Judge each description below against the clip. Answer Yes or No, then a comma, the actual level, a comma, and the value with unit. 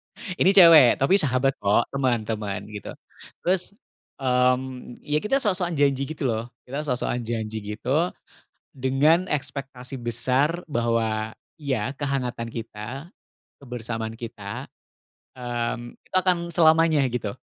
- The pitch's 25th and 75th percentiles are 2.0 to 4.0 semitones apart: No, average, 4.5 semitones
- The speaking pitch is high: No, low, 130 Hz